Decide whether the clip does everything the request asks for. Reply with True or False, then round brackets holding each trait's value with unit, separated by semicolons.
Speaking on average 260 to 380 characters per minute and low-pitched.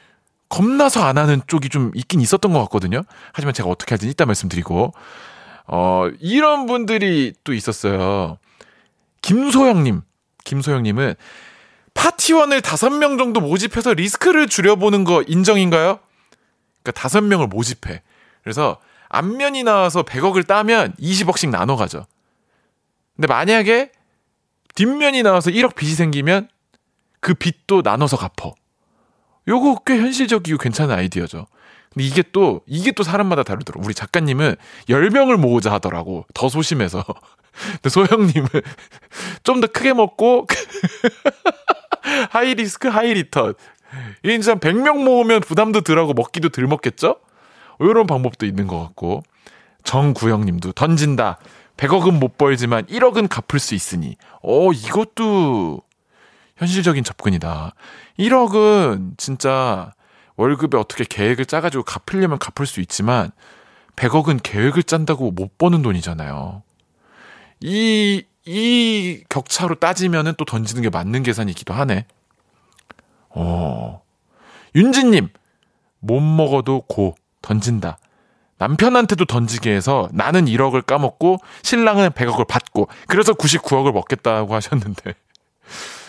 False (270 characters per minute; 160 Hz)